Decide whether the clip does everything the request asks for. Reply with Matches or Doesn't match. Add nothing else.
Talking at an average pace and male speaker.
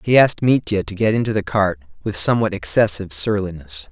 Matches